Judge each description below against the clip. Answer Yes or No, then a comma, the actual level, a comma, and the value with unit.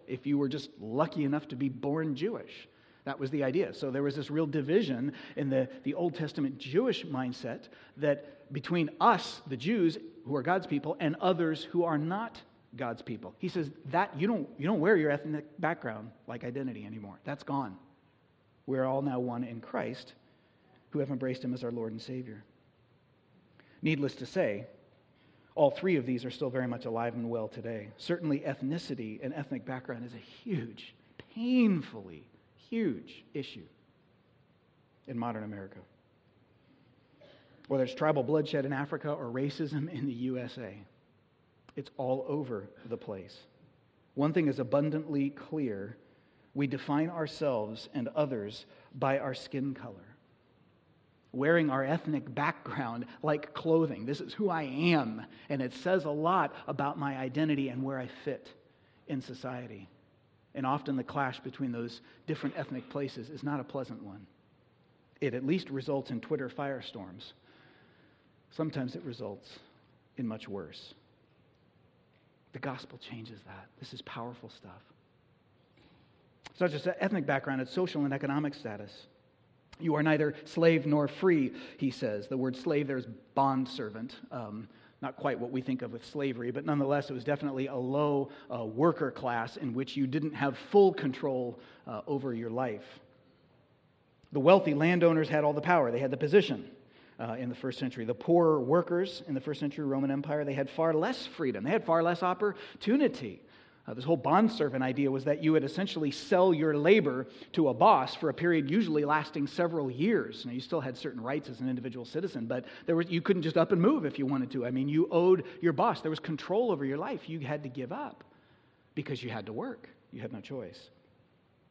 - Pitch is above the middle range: No, medium, 140 Hz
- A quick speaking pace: No, average, 175 wpm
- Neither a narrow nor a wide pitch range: Yes, average, 3.5 semitones